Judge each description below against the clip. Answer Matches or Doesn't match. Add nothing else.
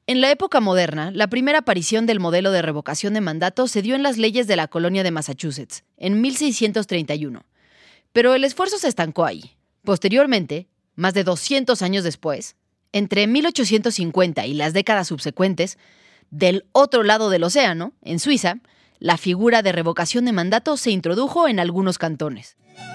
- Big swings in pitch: Matches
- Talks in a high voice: Matches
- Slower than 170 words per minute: Matches